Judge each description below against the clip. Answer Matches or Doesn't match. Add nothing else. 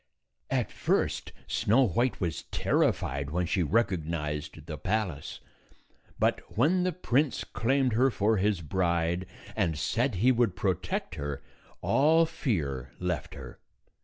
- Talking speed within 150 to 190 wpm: Doesn't match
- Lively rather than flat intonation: Matches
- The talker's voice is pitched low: Matches